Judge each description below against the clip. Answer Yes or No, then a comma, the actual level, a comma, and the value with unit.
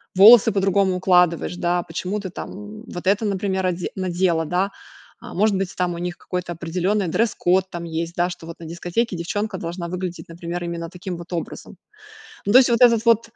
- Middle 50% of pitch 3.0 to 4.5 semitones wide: No, narrow, 2.5 semitones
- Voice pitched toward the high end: No, medium, 180 Hz